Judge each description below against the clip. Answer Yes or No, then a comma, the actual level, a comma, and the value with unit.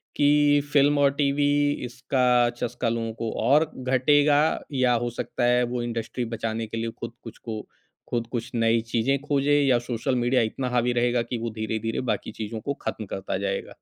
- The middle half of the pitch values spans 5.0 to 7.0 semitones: No, average, 3.3 semitones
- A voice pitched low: Yes, low, 120 Hz